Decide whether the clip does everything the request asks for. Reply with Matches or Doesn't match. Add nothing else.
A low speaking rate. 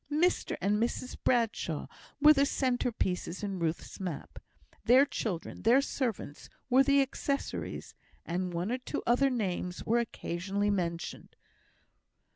Matches